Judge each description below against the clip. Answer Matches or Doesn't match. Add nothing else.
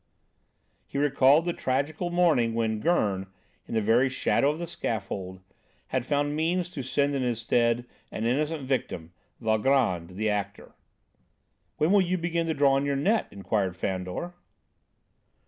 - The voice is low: Matches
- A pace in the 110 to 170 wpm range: Matches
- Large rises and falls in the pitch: Matches